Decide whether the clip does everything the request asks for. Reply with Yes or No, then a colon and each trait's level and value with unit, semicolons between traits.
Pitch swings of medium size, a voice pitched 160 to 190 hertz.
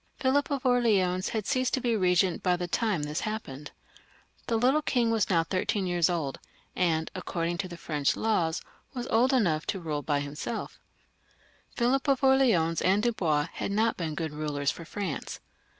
No: wide, 6.3 semitones; medium, 185 Hz